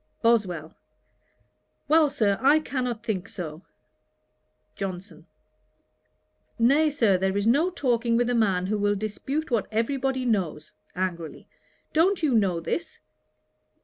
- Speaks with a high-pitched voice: Yes, high, 225 Hz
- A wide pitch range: Yes, wide, 6.1 semitones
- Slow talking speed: Yes, slow, 125 wpm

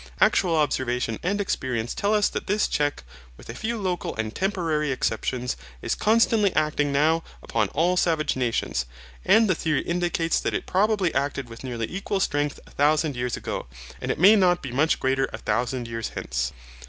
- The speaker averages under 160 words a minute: No, average, 180 wpm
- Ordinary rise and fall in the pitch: No, wide, 6.6 semitones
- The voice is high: No, medium, 150 Hz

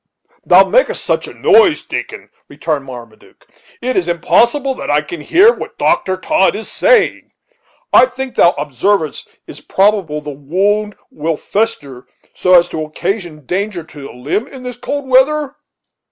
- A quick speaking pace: No, average, 160 wpm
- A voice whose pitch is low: No, high, 190 Hz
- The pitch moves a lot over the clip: Yes, wide, 8.9 semitones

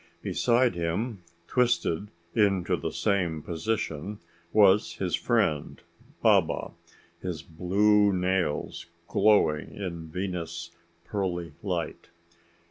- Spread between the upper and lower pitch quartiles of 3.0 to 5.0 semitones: Yes, average, 3.6 semitones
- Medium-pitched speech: No, very low, 95 Hz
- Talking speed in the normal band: No, slow, 90 wpm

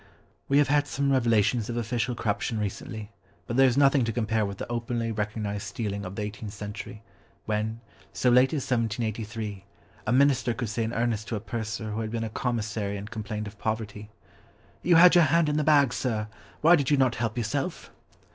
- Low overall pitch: Yes, low, 115 Hz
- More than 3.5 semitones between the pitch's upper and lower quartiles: No, average, 3.2 semitones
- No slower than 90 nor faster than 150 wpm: No, average, 200 wpm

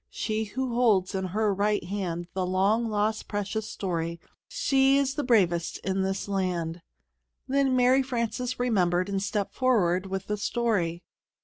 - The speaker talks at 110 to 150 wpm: Yes, average, 145 wpm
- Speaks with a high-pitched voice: Yes, high, 205 Hz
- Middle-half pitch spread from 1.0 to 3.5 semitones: No, average, 4.4 semitones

